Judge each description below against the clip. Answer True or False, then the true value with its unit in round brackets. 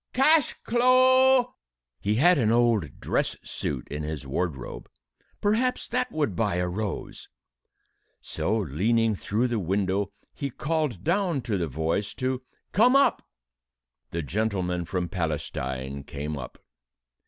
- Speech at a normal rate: False (130 wpm)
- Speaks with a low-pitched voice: True (105 Hz)